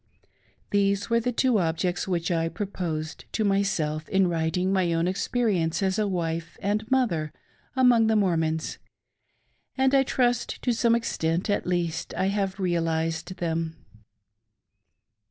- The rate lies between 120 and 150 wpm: Yes, slow, 135 wpm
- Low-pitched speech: No, medium, 185 Hz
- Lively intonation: No, average, 4.5 semitones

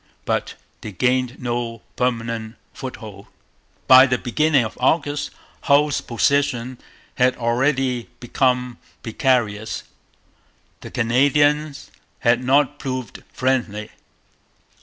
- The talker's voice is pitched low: Yes, low, 125 Hz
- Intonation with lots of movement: No, narrow, 2.5 semitones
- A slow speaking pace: Yes, slow, 95 wpm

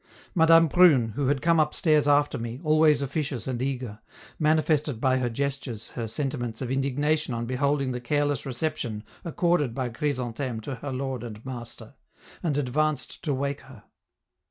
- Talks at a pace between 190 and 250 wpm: No, average, 155 wpm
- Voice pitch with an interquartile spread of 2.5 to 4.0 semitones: Yes, average, 3.4 semitones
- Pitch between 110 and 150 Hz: Yes, low, 135 Hz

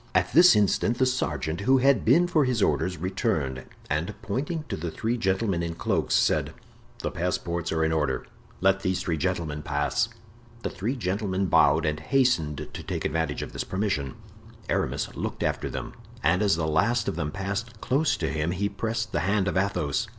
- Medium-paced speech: Yes, average, 185 wpm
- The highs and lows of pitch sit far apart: Yes, wide, 6.0 semitones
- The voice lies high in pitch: No, very low, 95 Hz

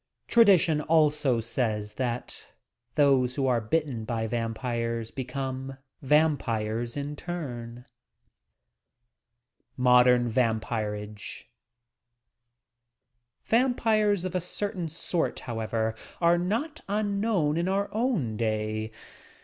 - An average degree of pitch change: No, wide, 6.9 semitones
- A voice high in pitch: No, low, 130 Hz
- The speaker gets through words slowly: Yes, slow, 95 wpm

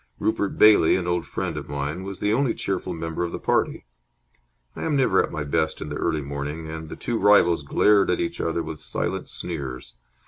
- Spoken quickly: Yes, fast, 210 wpm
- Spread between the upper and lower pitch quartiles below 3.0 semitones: No, average, 5.1 semitones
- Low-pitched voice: Yes, very low, 85 Hz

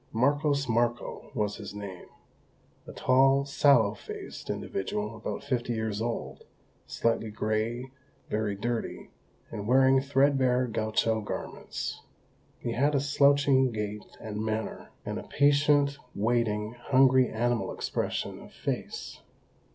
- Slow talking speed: Yes, slow, 120 wpm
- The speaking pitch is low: Yes, low, 120 Hz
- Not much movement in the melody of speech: No, average, 3.8 semitones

